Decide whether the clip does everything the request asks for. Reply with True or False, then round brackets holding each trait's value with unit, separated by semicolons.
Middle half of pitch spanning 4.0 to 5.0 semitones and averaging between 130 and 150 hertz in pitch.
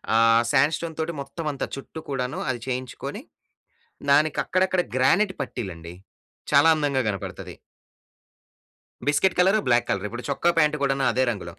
True (4.6 semitones; 140 Hz)